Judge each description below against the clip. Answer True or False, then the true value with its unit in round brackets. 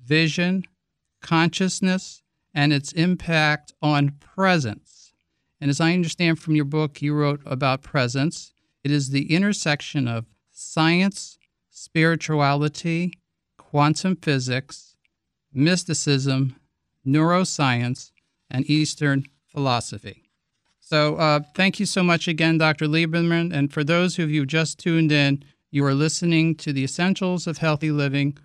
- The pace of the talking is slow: True (125 wpm)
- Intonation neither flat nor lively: True (3.0 semitones)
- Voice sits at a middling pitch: True (150 Hz)